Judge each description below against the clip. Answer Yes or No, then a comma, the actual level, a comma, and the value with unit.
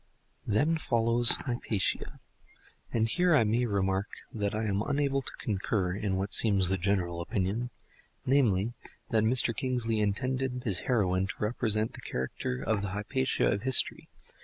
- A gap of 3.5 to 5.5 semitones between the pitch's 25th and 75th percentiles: Yes, average, 3.9 semitones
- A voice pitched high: No, low, 110 Hz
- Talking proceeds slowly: No, average, 145 wpm